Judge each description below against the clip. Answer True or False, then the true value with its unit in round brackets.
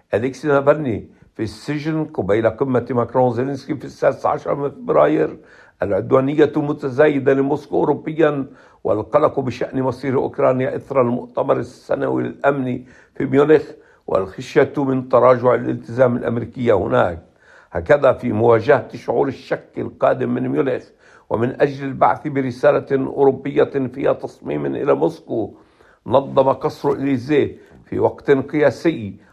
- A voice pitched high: False (135 Hz)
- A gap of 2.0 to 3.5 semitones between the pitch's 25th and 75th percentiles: True (2.7 semitones)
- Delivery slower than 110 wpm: False (115 wpm)